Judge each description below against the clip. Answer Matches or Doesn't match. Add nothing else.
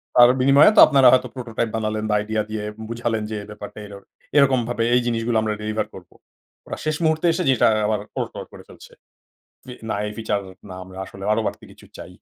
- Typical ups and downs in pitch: Matches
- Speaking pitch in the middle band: Doesn't match